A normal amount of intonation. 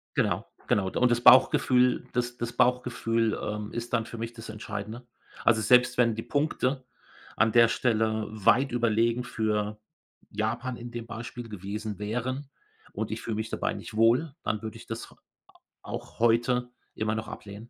No: narrow, 2.1 semitones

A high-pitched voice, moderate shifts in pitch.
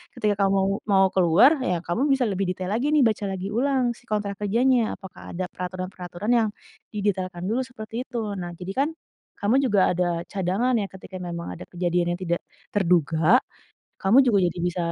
Yes: high, 195 Hz; average, 4.3 semitones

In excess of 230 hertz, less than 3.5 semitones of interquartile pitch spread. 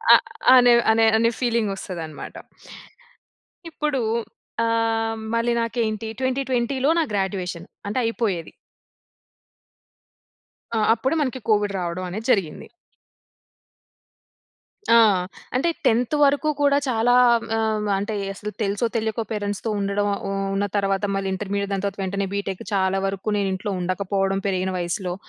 No: high, 210 Hz; average, 3.0 semitones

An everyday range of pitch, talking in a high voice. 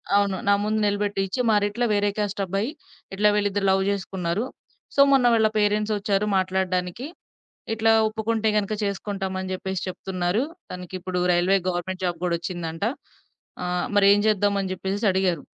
No: narrow, 2.1 semitones; high, 195 Hz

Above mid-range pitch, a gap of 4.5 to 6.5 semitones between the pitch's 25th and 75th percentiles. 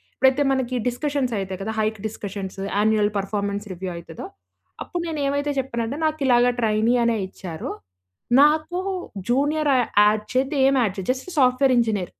Yes: high, 235 Hz; average, 4.9 semitones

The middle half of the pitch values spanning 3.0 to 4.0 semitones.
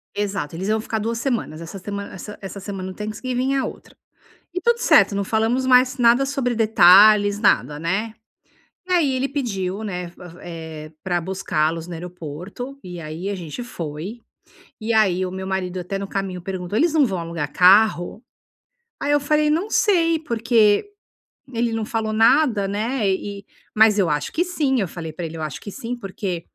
No: average, 5.1 semitones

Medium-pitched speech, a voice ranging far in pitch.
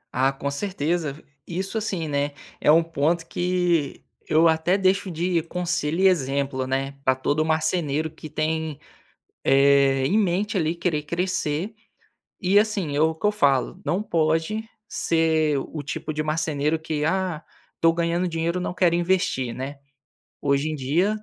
No: medium, 160 Hz; average, 3.6 semitones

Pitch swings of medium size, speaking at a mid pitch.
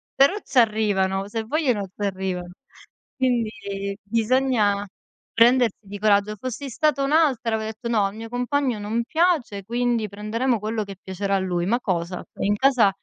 No: average, 3.8 semitones; high, 220 Hz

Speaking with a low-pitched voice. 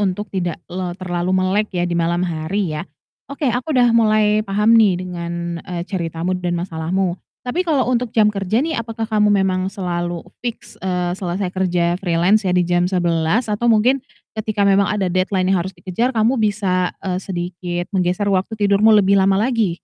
No: high, 190 Hz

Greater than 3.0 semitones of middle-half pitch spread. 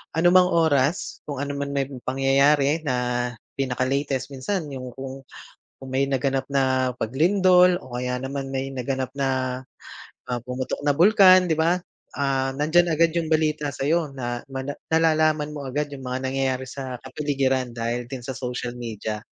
No: average, 2.7 semitones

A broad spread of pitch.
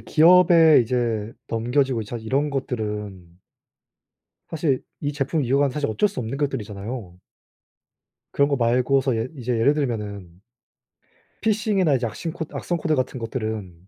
No: average, 4.8 semitones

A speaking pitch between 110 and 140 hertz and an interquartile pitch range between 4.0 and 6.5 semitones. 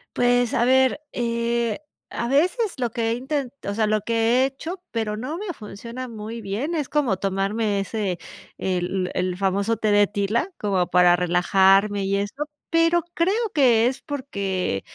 No: high, 225 Hz; average, 4.9 semitones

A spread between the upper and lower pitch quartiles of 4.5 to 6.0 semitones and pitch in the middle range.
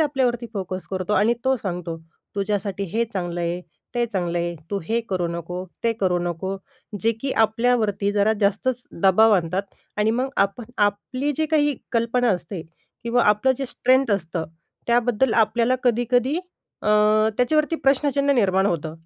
No: average, 4.8 semitones; high, 215 Hz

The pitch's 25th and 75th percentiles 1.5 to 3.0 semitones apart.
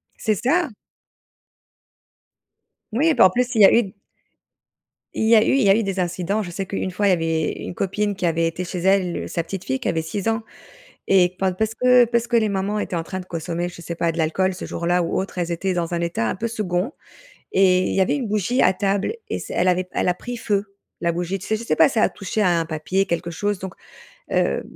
No: average, 3.4 semitones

